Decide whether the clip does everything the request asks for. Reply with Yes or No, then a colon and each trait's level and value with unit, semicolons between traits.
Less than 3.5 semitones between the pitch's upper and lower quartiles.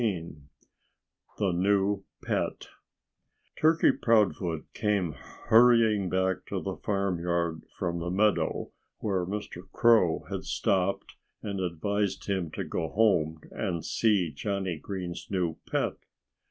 Yes: average, 3.1 semitones